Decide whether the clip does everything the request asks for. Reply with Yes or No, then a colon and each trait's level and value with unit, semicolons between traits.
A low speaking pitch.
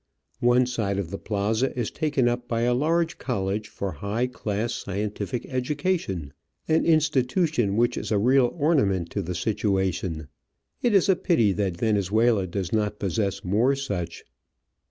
Yes: low, 110 Hz